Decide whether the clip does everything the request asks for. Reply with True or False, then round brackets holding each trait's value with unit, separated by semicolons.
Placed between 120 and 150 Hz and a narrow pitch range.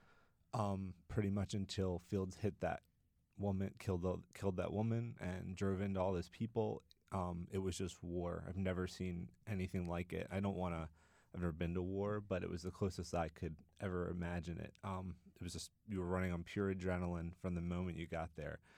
False (90 Hz; 2.0 semitones)